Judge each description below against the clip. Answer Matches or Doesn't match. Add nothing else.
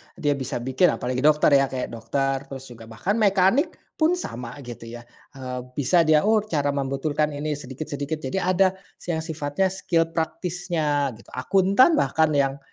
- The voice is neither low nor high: Matches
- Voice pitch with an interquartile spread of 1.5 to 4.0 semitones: Doesn't match